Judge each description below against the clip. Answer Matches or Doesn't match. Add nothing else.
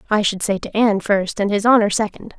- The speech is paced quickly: Matches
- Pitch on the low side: Doesn't match